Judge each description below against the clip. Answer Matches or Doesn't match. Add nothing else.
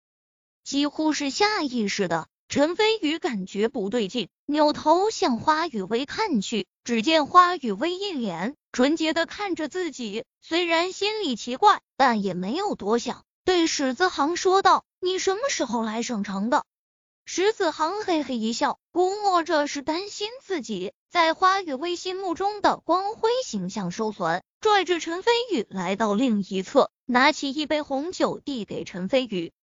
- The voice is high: Matches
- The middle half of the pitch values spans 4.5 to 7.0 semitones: Doesn't match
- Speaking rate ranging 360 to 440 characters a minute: Doesn't match